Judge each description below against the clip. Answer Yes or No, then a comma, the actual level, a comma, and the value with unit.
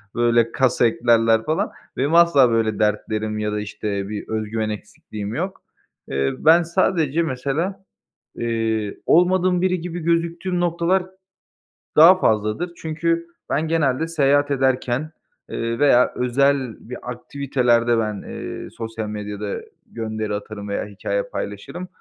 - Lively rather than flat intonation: Yes, wide, 7.2 semitones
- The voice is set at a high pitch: No, low, 125 Hz